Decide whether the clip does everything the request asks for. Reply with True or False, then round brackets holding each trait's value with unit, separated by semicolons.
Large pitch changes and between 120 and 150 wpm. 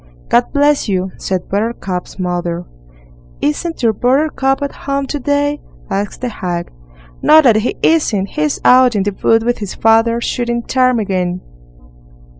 True (5.9 semitones; 145 wpm)